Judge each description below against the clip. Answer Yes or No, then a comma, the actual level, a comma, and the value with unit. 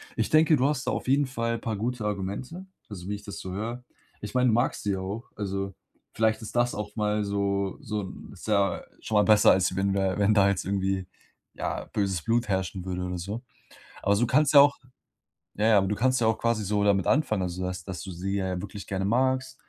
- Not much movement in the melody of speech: No, average, 3.3 semitones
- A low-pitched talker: Yes, low, 105 Hz